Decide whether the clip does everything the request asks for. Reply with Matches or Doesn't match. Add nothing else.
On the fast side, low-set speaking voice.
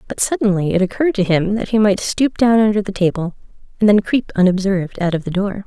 Doesn't match